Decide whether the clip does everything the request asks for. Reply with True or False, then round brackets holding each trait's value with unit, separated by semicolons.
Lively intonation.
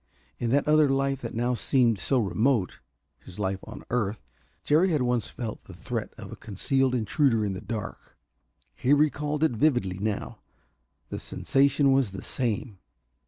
False (4.3 semitones)